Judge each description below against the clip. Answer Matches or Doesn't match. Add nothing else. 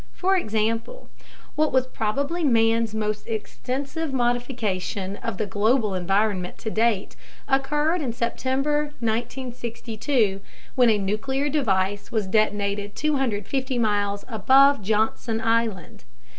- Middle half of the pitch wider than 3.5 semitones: Matches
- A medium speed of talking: Doesn't match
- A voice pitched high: Matches